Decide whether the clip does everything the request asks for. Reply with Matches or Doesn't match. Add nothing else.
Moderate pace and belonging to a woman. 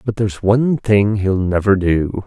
Doesn't match